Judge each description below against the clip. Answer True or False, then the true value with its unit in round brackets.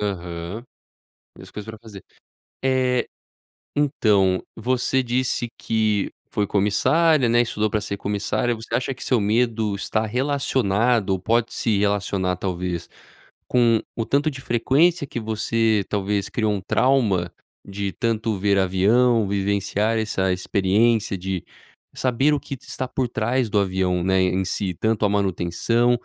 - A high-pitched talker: False (110 Hz)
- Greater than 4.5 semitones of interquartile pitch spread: False (3.6 semitones)